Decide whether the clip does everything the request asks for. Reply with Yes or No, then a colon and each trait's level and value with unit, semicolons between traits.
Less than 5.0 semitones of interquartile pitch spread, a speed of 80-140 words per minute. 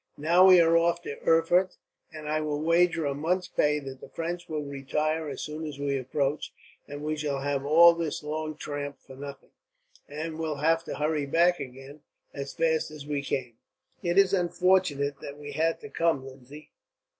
No: average, 2.7 semitones; average, 190 wpm